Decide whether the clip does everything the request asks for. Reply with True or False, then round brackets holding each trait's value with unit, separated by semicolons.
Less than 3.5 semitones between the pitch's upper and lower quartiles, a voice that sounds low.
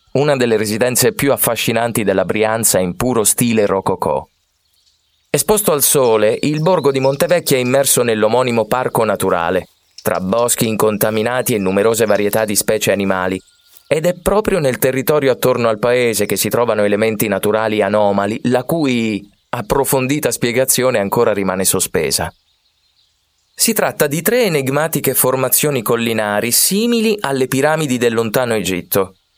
False (5.5 semitones; 115 Hz)